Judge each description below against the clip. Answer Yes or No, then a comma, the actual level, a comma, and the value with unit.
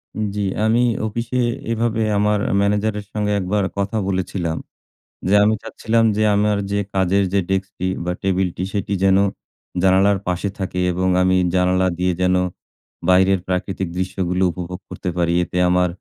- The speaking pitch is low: Yes, very low, 95 Hz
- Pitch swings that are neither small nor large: No, narrow, 2.2 semitones